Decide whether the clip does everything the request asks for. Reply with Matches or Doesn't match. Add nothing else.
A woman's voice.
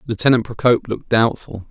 Doesn't match